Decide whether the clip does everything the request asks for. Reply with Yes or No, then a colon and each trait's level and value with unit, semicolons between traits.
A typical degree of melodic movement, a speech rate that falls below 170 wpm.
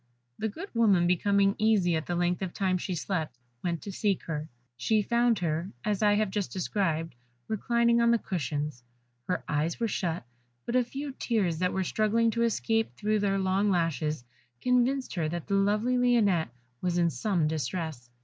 No: average, 4.7 semitones; average, 180 wpm